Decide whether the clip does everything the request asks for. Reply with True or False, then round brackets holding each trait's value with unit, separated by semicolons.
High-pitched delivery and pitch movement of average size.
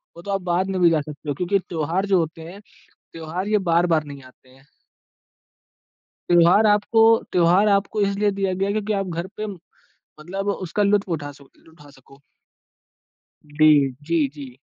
False (175 Hz; 4.3 semitones)